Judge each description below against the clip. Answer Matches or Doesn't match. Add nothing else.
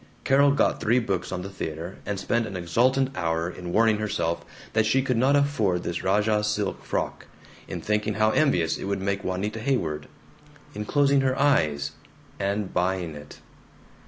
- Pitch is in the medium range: Doesn't match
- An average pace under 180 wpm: Matches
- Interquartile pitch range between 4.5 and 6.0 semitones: Matches